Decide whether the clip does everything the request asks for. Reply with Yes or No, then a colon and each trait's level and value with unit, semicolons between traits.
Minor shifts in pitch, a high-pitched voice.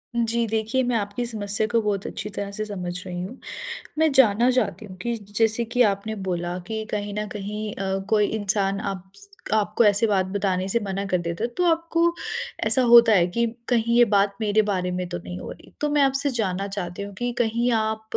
No: average, 3.0 semitones; high, 210 Hz